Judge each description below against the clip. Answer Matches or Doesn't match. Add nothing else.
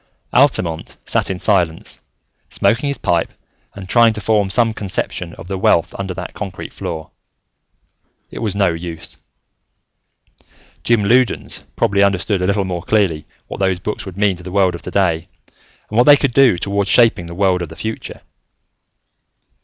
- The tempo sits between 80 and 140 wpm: Doesn't match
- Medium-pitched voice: Doesn't match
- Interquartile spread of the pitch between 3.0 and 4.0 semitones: Matches